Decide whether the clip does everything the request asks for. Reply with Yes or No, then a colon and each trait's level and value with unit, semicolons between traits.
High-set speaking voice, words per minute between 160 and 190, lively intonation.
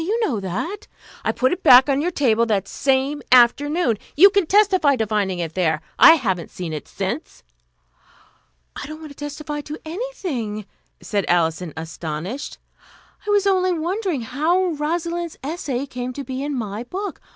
Yes: very high, 280 Hz; average, 165 wpm; wide, 8.0 semitones